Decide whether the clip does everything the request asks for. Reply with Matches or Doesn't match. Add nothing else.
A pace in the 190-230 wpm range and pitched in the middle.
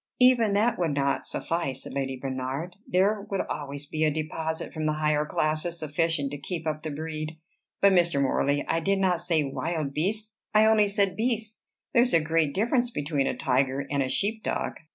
Matches